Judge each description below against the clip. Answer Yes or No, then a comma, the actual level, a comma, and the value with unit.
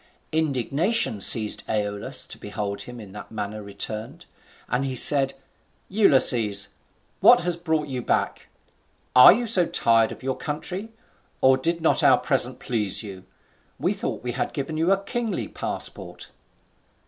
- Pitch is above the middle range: No, low, 130 Hz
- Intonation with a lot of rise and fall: Yes, wide, 7.2 semitones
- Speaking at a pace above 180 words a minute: No, average, 150 wpm